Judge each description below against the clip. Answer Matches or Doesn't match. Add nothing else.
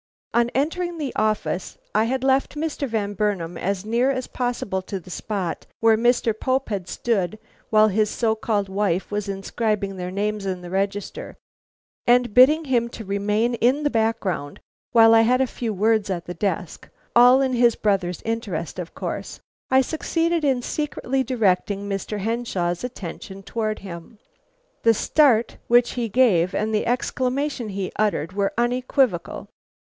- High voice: Matches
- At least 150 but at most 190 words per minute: Matches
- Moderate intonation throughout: Matches